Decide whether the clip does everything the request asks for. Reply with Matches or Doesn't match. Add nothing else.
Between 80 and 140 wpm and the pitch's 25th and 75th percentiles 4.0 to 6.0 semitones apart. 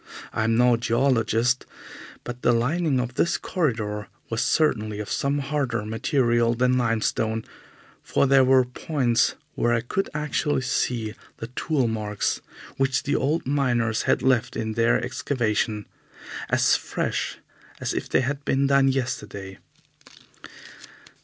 Doesn't match